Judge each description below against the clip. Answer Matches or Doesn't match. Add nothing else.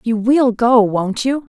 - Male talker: Doesn't match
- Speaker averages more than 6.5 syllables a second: Doesn't match